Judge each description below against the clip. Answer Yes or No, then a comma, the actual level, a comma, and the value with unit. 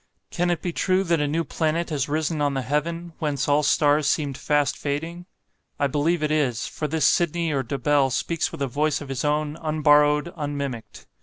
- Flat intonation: Yes, narrow, 2.2 semitones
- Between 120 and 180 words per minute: No, average, 200 wpm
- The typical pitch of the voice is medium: Yes, medium, 150 Hz